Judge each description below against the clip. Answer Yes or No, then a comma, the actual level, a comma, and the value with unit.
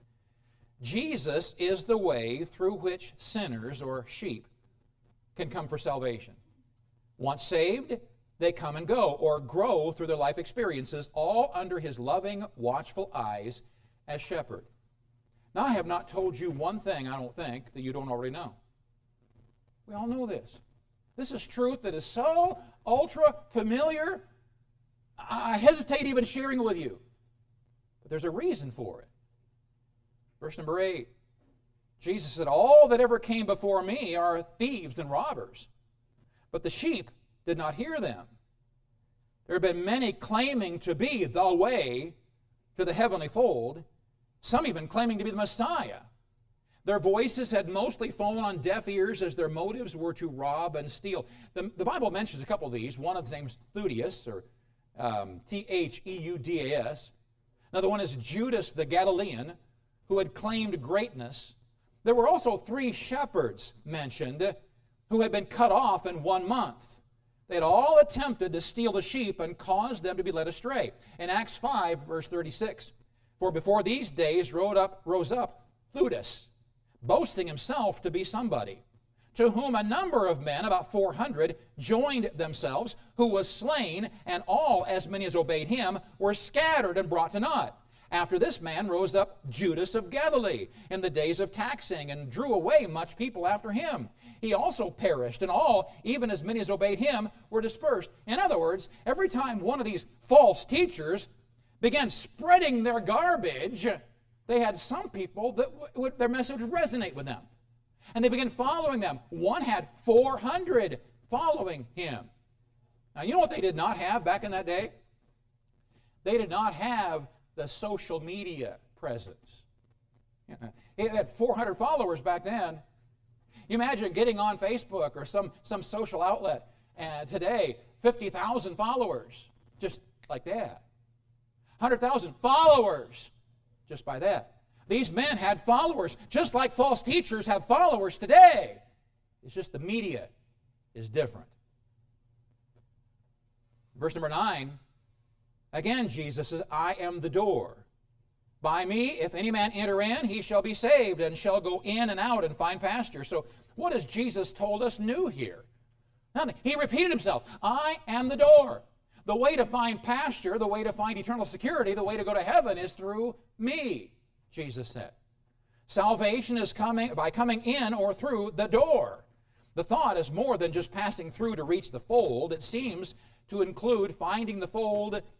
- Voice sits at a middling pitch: Yes, medium, 170 Hz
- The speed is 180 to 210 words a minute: No, average, 160 wpm